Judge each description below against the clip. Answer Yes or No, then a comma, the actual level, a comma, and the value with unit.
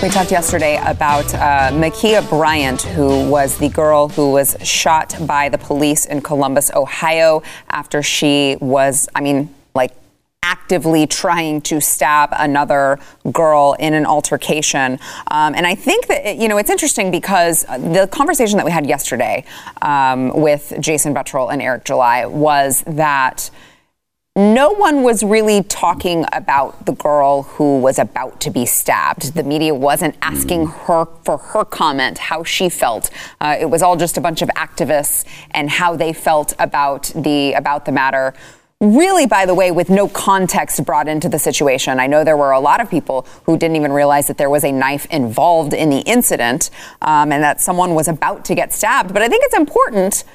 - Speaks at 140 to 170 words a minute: No, average, 180 wpm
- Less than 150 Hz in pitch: No, medium, 155 Hz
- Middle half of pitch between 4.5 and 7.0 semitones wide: No, average, 3.4 semitones